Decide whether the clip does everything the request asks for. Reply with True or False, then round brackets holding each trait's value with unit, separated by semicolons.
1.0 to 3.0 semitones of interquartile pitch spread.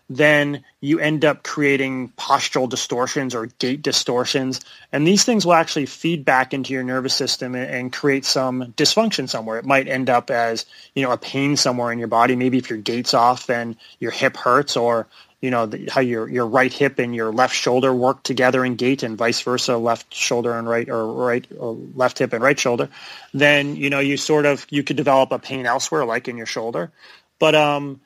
True (2.7 semitones)